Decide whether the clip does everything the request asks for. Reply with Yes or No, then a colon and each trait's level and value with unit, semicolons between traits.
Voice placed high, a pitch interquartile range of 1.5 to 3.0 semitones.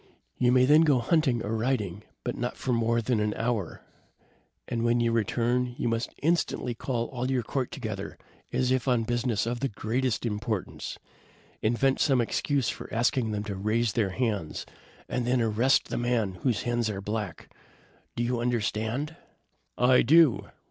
No: low, 120 Hz; narrow, 2.4 semitones